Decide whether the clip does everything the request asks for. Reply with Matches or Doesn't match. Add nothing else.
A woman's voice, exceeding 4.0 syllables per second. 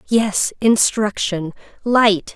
Doesn't match